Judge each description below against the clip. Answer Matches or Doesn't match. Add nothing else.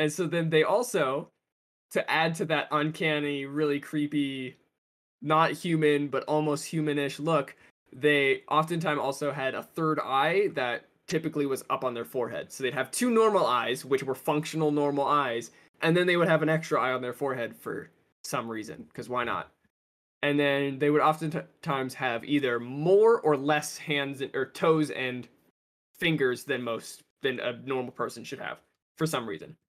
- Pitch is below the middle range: Doesn't match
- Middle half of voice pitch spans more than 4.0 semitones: Doesn't match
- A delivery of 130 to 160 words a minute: Doesn't match